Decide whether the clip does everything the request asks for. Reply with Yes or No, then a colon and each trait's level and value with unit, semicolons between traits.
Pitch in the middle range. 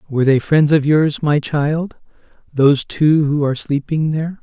Yes: medium, 150 Hz